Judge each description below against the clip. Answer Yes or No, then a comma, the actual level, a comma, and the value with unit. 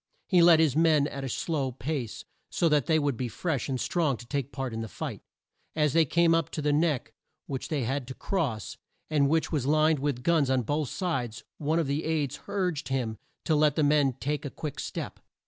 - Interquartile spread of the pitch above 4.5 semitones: No, average, 3.2 semitones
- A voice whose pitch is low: No, medium, 145 Hz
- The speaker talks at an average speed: No, fast, 220 wpm